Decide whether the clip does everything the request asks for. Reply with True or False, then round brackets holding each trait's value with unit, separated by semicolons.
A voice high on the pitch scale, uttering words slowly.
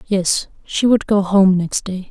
False (195 Hz; 200 wpm)